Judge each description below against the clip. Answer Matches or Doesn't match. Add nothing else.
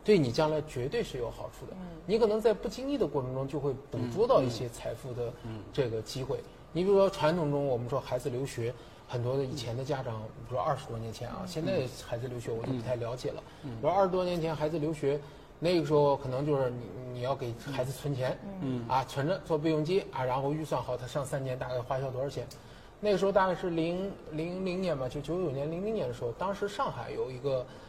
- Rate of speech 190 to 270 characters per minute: Doesn't match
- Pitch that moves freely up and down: Doesn't match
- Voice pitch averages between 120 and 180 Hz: Matches